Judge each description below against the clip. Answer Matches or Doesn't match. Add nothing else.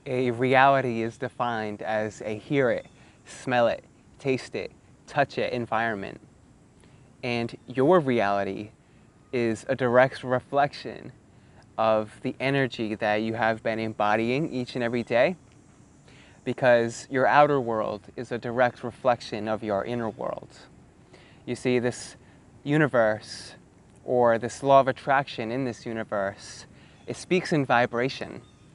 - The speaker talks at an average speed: Doesn't match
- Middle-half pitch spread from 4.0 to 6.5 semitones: Doesn't match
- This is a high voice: Doesn't match